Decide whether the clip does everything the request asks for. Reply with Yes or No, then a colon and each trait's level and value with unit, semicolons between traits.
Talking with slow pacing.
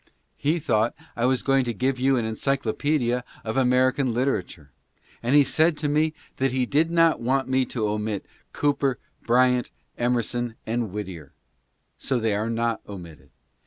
No: average, 160 wpm